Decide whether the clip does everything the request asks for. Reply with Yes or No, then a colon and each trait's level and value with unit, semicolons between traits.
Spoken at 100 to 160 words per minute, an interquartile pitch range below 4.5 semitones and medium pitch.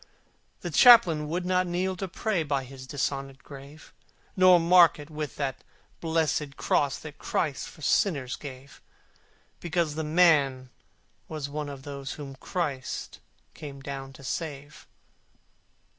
Yes: slow, 135 wpm; average, 3.5 semitones; medium, 150 Hz